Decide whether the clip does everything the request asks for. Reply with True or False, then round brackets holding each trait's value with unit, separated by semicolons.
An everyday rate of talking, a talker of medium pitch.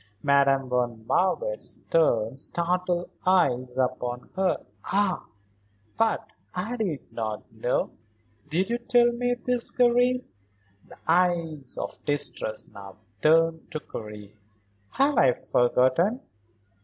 False (110 wpm; 165 Hz)